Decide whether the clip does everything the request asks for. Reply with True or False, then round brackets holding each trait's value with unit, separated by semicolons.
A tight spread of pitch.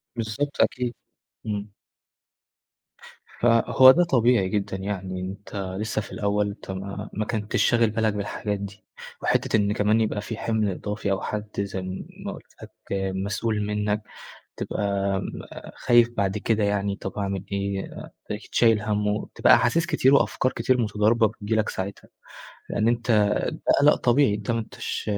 True (2.2 semitones)